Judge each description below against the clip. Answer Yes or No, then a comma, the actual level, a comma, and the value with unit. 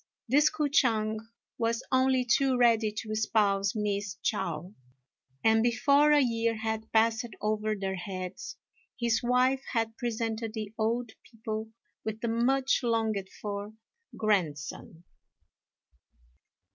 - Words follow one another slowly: Yes, slow, 120 wpm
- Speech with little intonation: Yes, narrow, 2.3 semitones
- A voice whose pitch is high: Yes, high, 225 Hz